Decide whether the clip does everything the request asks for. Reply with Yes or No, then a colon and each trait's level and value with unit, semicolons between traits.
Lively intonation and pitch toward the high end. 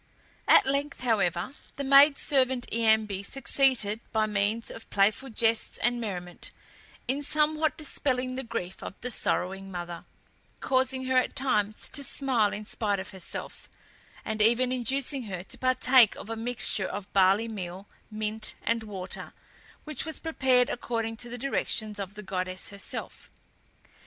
No: average, 4.4 semitones; high, 225 Hz